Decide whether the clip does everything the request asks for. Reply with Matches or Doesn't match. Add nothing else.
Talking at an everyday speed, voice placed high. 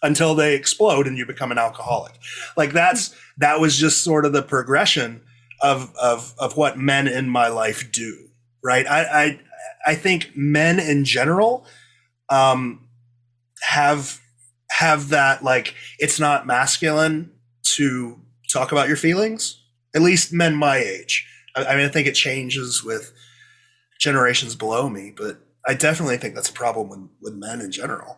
Doesn't match